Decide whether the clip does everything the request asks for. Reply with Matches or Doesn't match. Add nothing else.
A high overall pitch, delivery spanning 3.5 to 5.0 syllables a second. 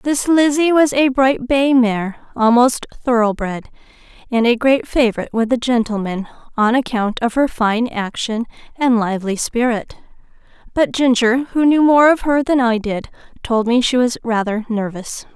Matches